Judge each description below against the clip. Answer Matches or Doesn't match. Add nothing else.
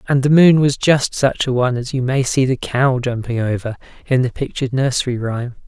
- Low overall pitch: Matches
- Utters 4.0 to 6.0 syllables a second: Matches